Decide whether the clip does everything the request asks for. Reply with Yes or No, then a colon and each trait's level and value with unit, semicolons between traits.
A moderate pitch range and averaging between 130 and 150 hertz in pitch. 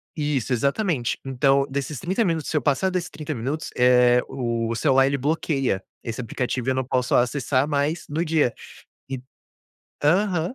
Yes: average, 3.8 semitones; medium, 140 Hz